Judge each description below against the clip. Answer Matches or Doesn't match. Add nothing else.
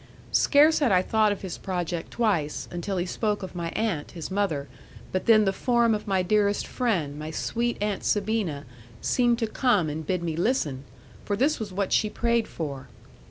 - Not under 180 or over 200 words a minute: Matches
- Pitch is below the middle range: Doesn't match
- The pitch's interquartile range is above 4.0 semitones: Matches